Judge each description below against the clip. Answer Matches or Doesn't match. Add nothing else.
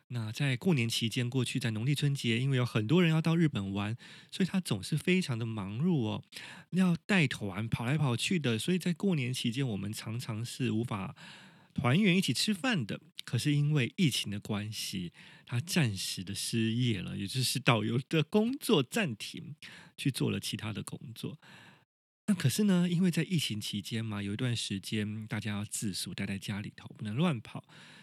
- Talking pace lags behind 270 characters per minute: Doesn't match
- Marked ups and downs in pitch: Matches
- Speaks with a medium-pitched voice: Doesn't match